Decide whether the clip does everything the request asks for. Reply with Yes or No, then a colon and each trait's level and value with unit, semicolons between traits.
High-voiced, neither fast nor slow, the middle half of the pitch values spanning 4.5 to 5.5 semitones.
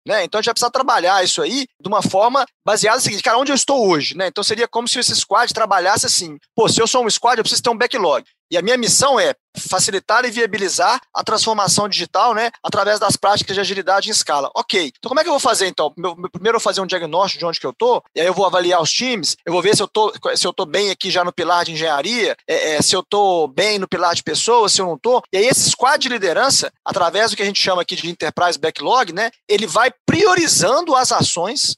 No: high, 205 Hz; fast, 260 wpm; average, 5.0 semitones